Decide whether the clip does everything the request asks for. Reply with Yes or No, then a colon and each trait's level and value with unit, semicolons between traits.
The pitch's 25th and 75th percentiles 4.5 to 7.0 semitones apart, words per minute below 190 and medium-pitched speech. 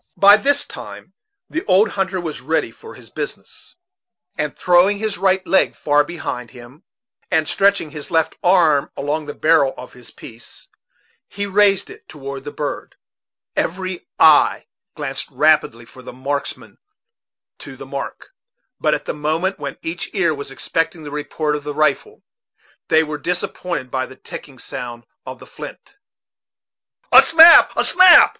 Yes: average, 4.8 semitones; average, 160 wpm; medium, 155 Hz